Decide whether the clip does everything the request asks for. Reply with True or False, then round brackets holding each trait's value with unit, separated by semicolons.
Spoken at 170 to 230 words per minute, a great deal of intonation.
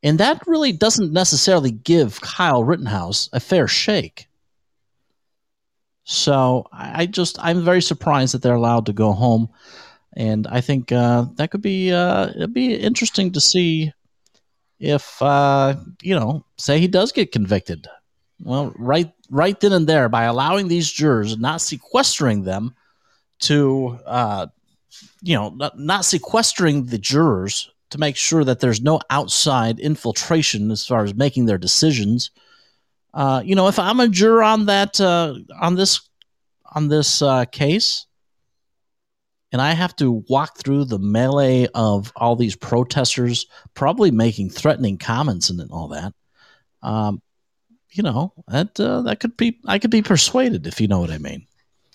False (155 wpm; 7.0 semitones)